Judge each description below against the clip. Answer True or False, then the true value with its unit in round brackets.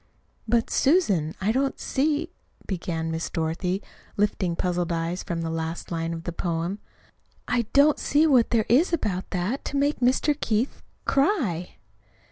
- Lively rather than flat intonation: True (8.2 semitones)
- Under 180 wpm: True (150 wpm)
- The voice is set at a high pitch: True (195 Hz)